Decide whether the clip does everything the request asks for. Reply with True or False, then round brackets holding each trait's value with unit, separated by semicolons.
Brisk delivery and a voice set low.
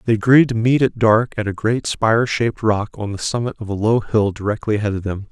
True (260 wpm; 110 Hz)